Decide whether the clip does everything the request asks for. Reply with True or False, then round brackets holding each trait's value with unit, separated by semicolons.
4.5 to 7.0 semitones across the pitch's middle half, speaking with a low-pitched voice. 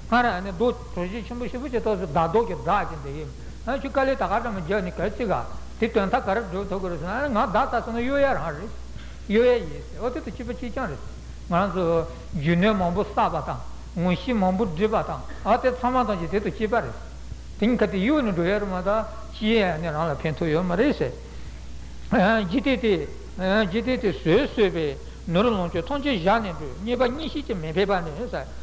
False (5.1 semitones; 210 Hz)